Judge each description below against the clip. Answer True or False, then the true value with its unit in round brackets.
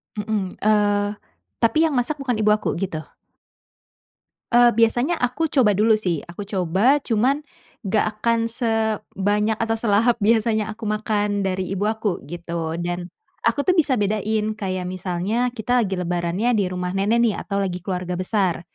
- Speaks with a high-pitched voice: True (210 Hz)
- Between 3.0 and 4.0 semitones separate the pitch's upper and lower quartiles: True (3.5 semitones)